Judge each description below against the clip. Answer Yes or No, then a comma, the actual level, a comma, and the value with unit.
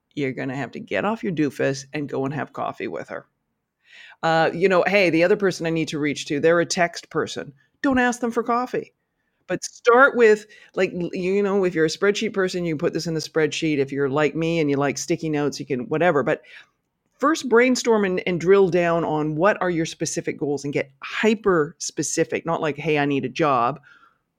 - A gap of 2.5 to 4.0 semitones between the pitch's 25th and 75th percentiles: No, average, 4.4 semitones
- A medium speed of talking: No, fast, 220 wpm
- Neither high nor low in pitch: Yes, medium, 165 Hz